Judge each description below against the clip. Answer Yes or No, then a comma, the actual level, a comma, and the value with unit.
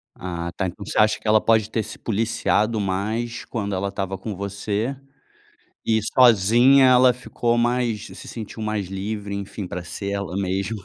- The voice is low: Yes, low, 105 Hz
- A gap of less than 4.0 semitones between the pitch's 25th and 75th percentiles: Yes, average, 2.7 semitones